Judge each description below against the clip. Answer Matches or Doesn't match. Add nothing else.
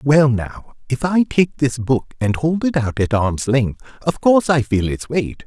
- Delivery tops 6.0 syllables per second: Doesn't match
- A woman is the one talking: Doesn't match